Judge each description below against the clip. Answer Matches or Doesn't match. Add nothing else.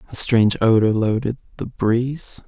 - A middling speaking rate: Matches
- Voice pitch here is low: Matches